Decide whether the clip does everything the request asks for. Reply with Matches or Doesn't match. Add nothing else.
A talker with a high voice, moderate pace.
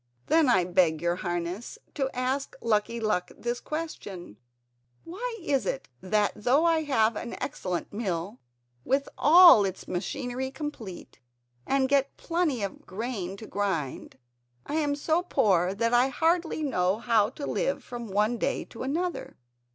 Matches